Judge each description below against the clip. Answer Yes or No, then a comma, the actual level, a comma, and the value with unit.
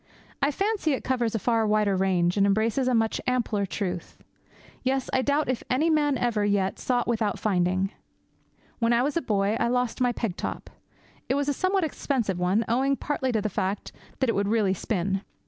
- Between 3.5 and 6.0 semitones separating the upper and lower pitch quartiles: Yes, average, 4.6 semitones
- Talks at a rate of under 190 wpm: No, average, 200 wpm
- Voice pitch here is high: Yes, high, 230 Hz